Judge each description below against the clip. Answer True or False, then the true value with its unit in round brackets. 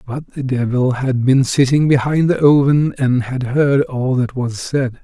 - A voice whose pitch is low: True (130 Hz)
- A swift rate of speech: False (190 wpm)